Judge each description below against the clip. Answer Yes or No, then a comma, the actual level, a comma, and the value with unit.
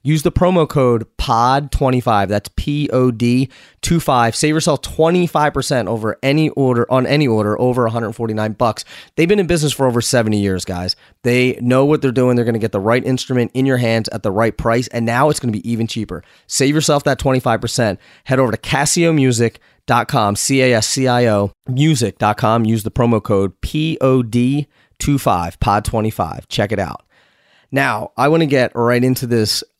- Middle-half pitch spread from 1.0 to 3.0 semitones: No, average, 3.7 semitones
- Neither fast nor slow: Yes, average, 175 wpm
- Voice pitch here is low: Yes, low, 125 Hz